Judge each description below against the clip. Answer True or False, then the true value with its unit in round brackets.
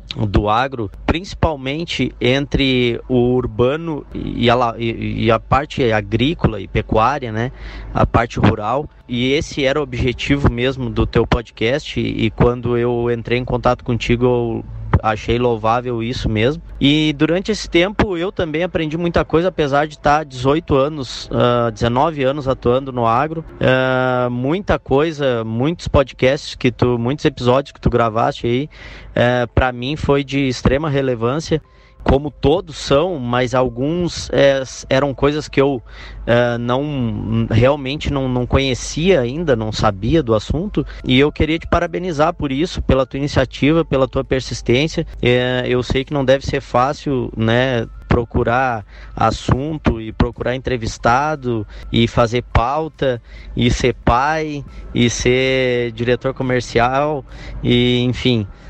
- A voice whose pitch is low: True (125 Hz)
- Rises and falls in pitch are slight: False (3.1 semitones)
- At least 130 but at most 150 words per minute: True (140 wpm)